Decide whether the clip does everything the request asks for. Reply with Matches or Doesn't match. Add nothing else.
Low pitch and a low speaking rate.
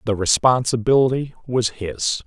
Matches